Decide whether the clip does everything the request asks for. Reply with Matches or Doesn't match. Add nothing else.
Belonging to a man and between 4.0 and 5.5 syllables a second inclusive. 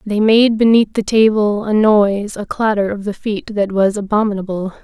Doesn't match